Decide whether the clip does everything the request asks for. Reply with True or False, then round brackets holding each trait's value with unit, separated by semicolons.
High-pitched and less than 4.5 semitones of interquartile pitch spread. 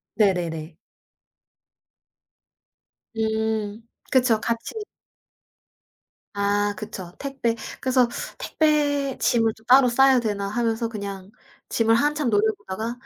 True (225 Hz; 3.5 semitones)